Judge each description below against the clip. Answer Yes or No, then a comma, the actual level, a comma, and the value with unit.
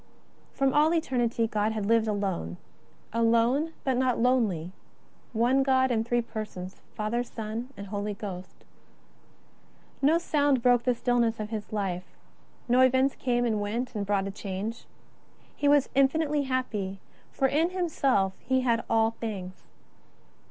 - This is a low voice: No, high, 230 Hz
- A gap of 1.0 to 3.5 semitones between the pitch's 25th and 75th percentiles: No, average, 3.9 semitones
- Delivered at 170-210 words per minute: No, average, 145 wpm